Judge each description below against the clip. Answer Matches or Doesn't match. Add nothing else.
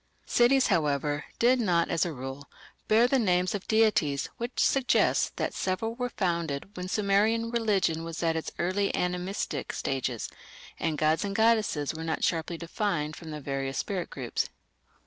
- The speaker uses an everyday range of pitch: Doesn't match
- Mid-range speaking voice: Matches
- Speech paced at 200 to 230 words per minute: Doesn't match